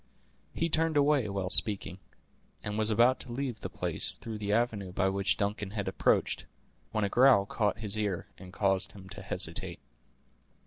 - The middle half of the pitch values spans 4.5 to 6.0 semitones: No, average, 3.3 semitones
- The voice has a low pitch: Yes, low, 105 Hz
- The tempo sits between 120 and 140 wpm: No, average, 175 wpm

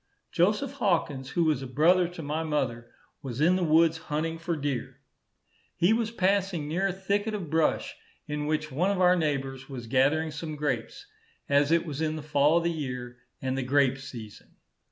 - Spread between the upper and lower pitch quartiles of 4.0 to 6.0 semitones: Yes, average, 4.3 semitones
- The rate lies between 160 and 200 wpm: Yes, average, 190 wpm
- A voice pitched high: No, medium, 155 Hz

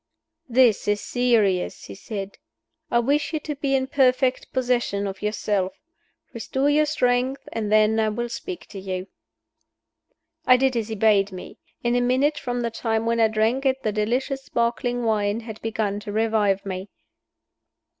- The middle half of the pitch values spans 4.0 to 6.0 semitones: No, average, 3.5 semitones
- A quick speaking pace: No, average, 165 wpm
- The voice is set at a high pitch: Yes, high, 230 Hz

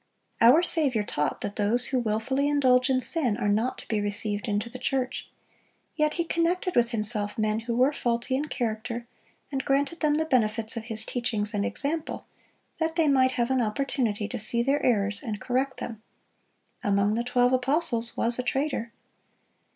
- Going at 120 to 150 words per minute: No, average, 180 wpm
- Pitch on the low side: No, high, 245 Hz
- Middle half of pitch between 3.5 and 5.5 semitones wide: Yes, average, 3.9 semitones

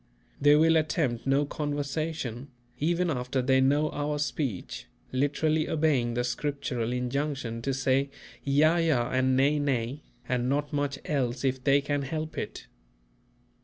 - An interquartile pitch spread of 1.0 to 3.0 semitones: Yes, narrow, 2.6 semitones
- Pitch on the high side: No, medium, 140 Hz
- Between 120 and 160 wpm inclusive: Yes, average, 140 wpm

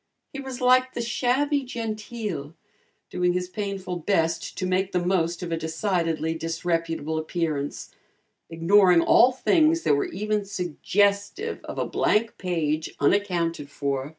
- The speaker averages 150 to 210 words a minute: No, slow, 135 wpm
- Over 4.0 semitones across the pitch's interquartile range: Yes, average, 4.6 semitones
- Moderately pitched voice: Yes, medium, 180 Hz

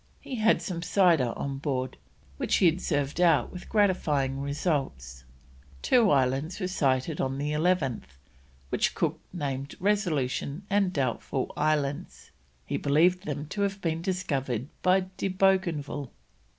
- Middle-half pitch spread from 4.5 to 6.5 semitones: Yes, average, 5.2 semitones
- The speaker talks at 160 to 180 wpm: No, slow, 135 wpm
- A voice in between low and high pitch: Yes, medium, 150 Hz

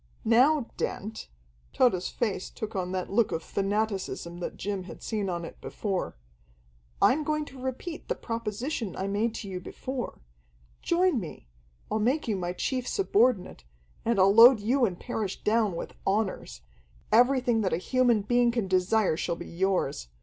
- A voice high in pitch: Yes, high, 215 Hz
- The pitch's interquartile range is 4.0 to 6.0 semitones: Yes, average, 4.5 semitones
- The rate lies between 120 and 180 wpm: Yes, average, 165 wpm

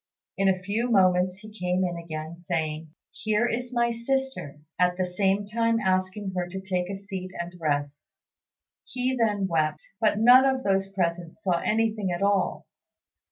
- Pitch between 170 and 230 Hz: Yes, high, 190 Hz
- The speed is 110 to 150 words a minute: No, average, 165 wpm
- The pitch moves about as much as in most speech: Yes, average, 3.6 semitones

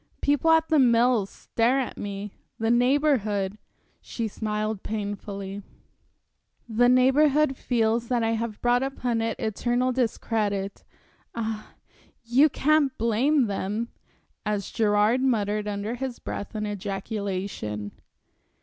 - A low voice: No, high, 225 Hz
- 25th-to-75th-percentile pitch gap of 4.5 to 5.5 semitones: No, average, 3.4 semitones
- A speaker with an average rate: No, slow, 115 wpm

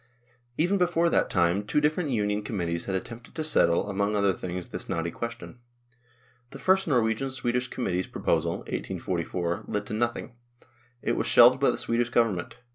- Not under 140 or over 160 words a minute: No, average, 170 wpm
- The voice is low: Yes, low, 115 Hz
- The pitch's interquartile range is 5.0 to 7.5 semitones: Yes, wide, 5.5 semitones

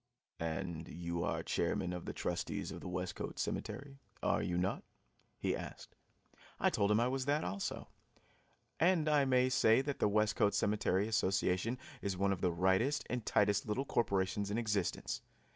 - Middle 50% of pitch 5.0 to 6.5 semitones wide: Yes, wide, 5.4 semitones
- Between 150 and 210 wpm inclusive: Yes, average, 165 wpm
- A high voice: No, low, 105 Hz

